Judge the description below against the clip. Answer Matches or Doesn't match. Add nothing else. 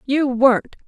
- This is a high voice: Matches